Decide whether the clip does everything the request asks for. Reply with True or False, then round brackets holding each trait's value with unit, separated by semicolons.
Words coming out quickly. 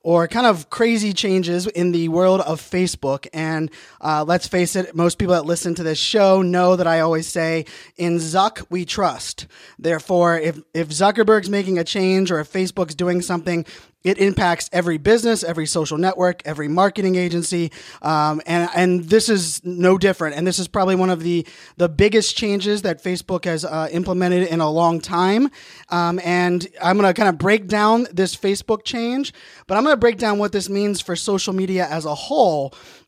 False (190 wpm)